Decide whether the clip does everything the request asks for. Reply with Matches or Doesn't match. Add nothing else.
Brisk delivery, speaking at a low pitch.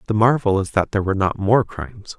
Matches